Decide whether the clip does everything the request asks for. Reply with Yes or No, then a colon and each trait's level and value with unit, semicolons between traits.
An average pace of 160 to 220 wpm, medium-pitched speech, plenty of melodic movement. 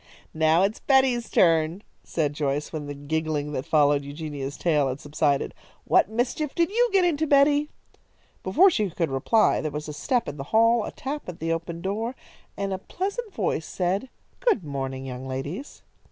Yes: average, 180 wpm; medium, 170 Hz; wide, 8.7 semitones